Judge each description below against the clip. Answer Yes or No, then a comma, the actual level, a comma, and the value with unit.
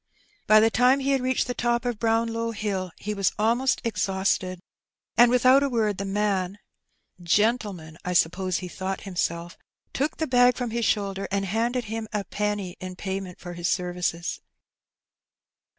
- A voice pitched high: Yes, high, 210 Hz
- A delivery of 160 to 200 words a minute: Yes, average, 165 wpm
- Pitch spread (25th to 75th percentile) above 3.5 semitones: Yes, average, 4.2 semitones